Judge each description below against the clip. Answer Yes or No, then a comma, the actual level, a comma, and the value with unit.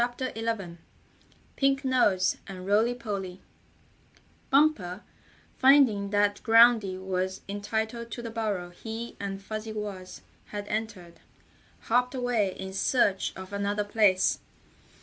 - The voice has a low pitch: No, high, 210 Hz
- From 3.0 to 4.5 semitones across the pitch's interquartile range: Yes, average, 3.4 semitones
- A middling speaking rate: No, slow, 115 wpm